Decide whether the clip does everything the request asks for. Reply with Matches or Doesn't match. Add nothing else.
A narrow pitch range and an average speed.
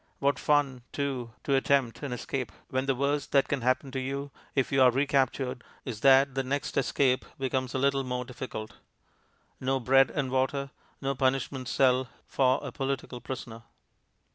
Matches